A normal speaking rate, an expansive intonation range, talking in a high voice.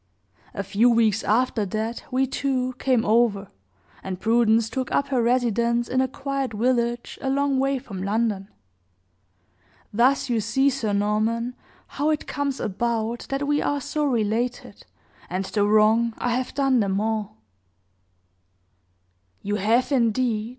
No: average, 145 wpm; average, 3.3 semitones; high, 235 Hz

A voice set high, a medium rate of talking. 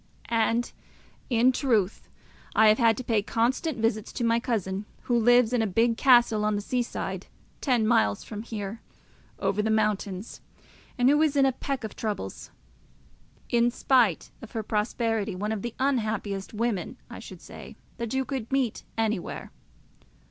Yes: high, 225 Hz; average, 165 wpm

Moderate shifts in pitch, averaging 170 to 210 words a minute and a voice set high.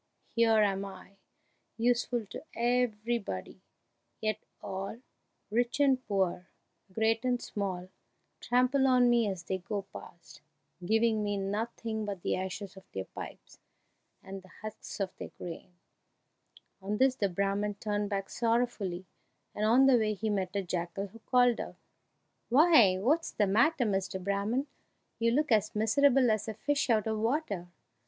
No: average, 3.6 semitones; average, 150 wpm; high, 215 Hz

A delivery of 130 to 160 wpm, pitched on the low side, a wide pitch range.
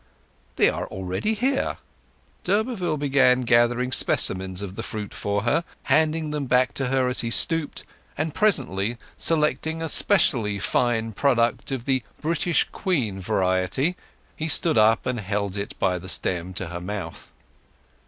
Yes: average, 150 wpm; low, 125 Hz; wide, 7.3 semitones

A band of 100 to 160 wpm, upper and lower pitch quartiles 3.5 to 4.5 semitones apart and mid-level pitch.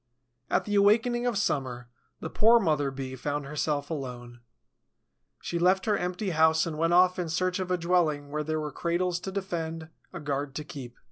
No: average, 190 wpm; average, 4.1 semitones; medium, 165 Hz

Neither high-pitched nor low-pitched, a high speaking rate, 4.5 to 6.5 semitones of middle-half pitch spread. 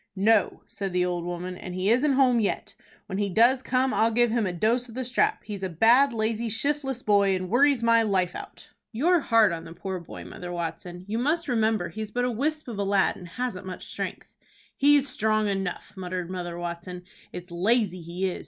No: high, 210 Hz; fast, 210 wpm; average, 5.0 semitones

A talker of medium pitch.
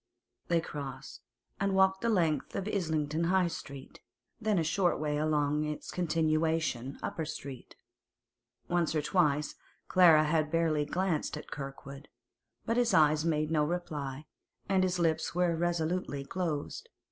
Yes: medium, 160 Hz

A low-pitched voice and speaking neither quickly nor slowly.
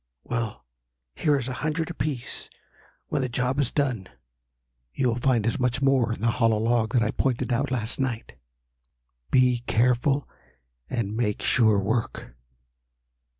Yes: low, 125 Hz; average, 150 wpm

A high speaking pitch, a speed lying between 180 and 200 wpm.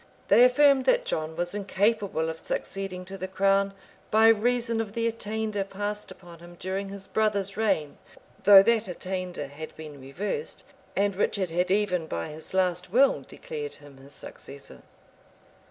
No: high, 195 Hz; average, 155 wpm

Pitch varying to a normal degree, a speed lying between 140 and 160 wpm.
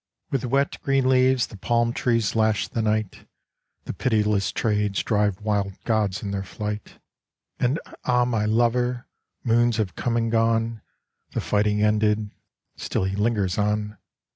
No: narrow, 2.2 semitones; average, 145 wpm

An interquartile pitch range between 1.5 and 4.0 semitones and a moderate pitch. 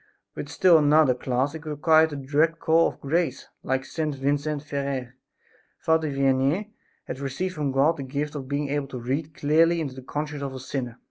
Yes: average, 2.7 semitones; medium, 145 Hz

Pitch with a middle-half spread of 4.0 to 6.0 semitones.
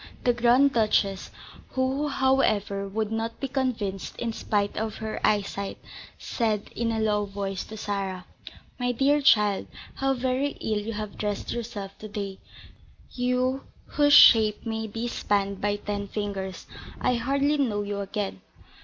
No: average, 3.6 semitones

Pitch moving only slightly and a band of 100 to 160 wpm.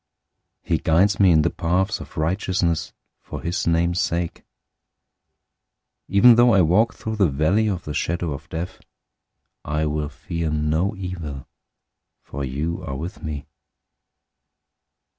No: average, 3.6 semitones; average, 140 wpm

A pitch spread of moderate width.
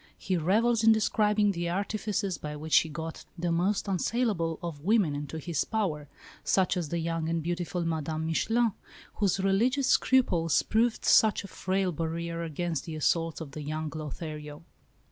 Yes: average, 4.2 semitones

